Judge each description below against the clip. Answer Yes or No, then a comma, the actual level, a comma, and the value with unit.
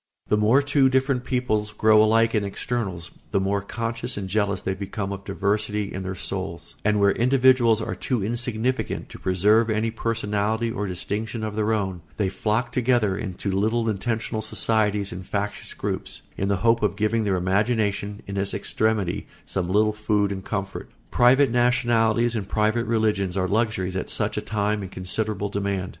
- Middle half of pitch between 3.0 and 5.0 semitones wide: No, narrow, 2.6 semitones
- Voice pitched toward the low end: Yes, low, 105 Hz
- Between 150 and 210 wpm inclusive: Yes, average, 175 wpm